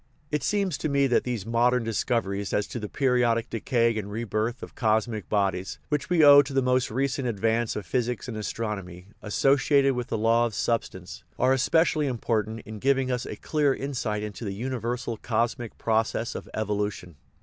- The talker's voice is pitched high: No, low, 115 Hz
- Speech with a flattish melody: No, average, 3.5 semitones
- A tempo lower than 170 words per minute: No, average, 185 wpm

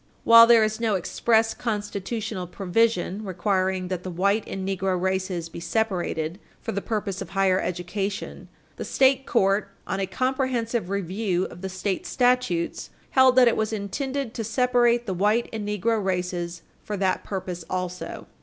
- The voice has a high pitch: Yes, high, 200 Hz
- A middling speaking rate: Yes, average, 160 wpm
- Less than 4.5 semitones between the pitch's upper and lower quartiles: Yes, average, 3.6 semitones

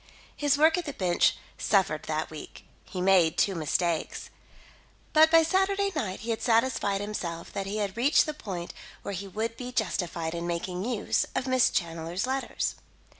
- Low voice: No, high, 200 Hz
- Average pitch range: No, wide, 6.8 semitones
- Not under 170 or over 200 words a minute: Yes, average, 175 wpm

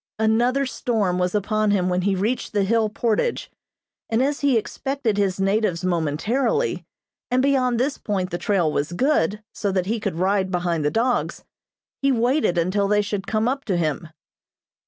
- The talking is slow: No, average, 175 wpm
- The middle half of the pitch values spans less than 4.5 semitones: No, average, 5.0 semitones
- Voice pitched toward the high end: Yes, high, 210 Hz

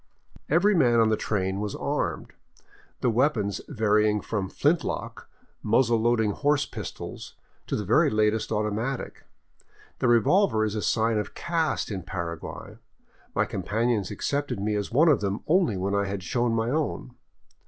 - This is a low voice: Yes, low, 110 Hz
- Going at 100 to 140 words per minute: No, average, 155 wpm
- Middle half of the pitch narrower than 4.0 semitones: No, average, 4.3 semitones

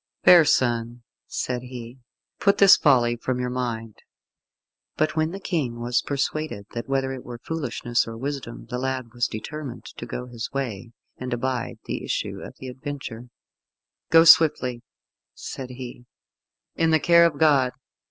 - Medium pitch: No, low, 125 Hz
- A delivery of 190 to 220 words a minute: No, average, 155 wpm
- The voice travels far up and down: No, average, 3.5 semitones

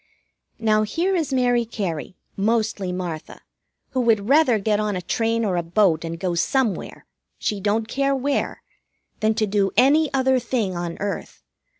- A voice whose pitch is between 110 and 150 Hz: No, high, 215 Hz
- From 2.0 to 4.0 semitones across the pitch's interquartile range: No, average, 4.6 semitones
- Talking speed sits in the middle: Yes, average, 165 wpm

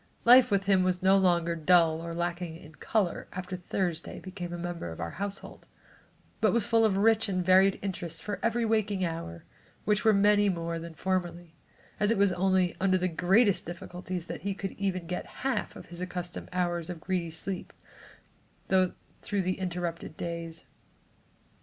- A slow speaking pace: No, average, 170 wpm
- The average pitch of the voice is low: No, medium, 185 Hz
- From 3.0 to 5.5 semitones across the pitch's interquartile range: No, narrow, 2.5 semitones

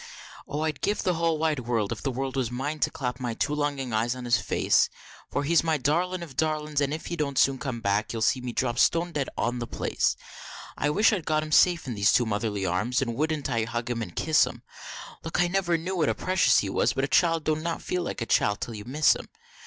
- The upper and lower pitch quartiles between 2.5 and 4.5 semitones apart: No, average, 4.9 semitones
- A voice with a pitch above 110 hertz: Yes, medium, 140 Hz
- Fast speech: Yes, fast, 260 wpm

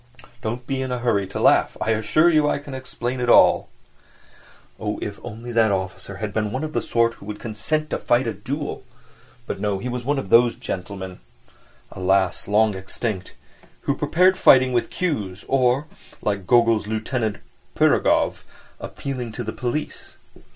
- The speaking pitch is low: Yes, low, 115 Hz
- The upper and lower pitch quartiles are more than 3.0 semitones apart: Yes, average, 4.1 semitones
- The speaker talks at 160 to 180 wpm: Yes, average, 165 wpm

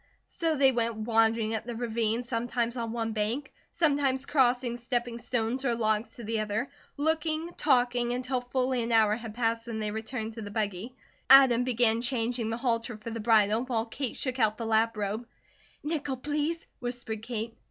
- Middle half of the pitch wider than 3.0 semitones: No, narrow, 2.4 semitones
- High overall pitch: Yes, high, 235 Hz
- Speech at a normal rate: Yes, average, 180 wpm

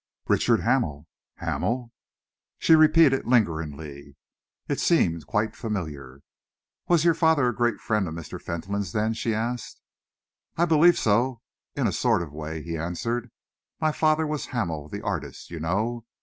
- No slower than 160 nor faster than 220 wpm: No, average, 150 wpm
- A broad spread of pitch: Yes, wide, 8.0 semitones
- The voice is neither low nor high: No, low, 110 Hz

